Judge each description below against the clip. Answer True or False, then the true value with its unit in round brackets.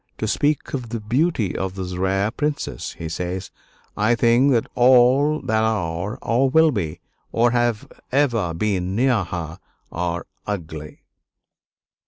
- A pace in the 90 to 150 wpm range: True (140 wpm)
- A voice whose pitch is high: False (110 Hz)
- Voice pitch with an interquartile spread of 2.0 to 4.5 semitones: False (5.5 semitones)